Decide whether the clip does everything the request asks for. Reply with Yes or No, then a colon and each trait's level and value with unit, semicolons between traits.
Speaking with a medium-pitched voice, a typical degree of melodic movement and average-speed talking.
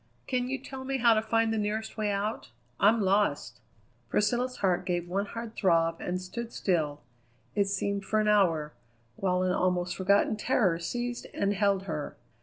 No: high, 200 Hz; average, 3.6 semitones; average, 175 wpm